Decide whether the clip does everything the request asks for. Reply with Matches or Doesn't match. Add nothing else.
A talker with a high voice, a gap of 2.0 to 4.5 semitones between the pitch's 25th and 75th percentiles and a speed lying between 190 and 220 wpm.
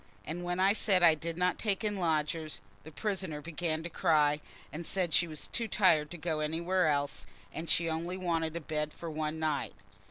Doesn't match